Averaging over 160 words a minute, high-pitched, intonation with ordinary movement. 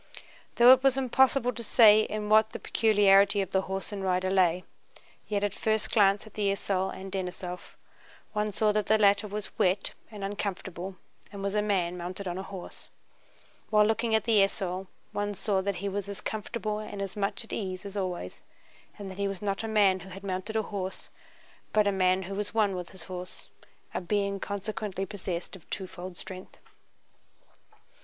No: average, 190 wpm; high, 200 Hz; narrow, 2.0 semitones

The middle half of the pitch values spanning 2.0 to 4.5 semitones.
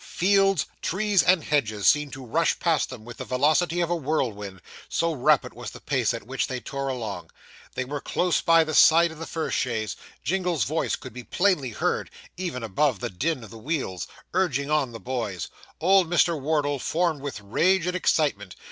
No: wide, 5.4 semitones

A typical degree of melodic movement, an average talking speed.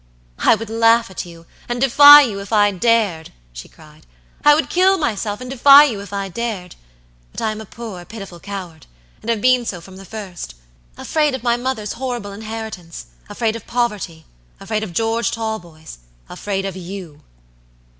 Yes: average, 4.0 semitones; average, 175 wpm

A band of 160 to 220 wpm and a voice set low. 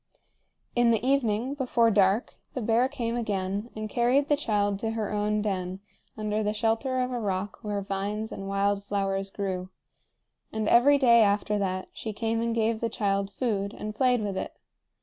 No: average, 180 wpm; high, 215 Hz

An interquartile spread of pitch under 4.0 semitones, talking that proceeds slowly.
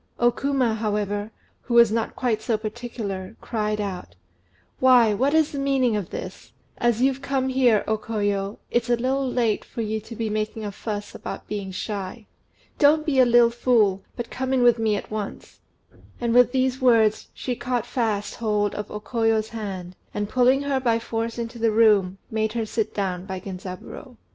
No: average, 2.9 semitones; average, 185 wpm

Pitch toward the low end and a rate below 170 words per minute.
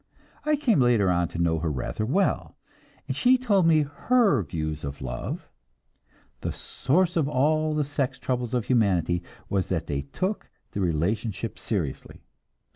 Yes: low, 120 Hz; average, 155 wpm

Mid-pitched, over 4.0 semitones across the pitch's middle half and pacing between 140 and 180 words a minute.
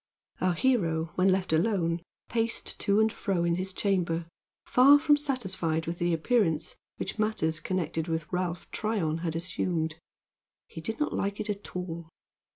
Yes: medium, 180 Hz; average, 4.4 semitones; average, 160 wpm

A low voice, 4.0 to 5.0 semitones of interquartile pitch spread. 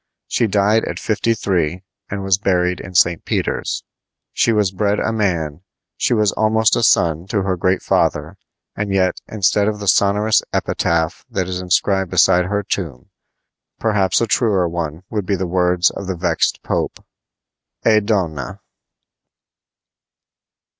No: very low, 95 Hz; average, 2.8 semitones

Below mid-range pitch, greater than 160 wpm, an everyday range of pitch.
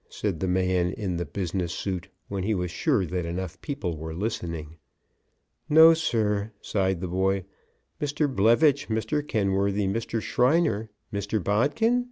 No: low, 100 Hz; average, 145 wpm; average, 4.1 semitones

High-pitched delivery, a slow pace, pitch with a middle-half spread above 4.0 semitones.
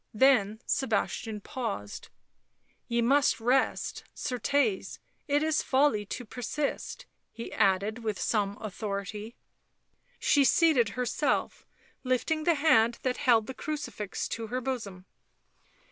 Yes: high, 240 Hz; slow, 115 wpm; average, 4.5 semitones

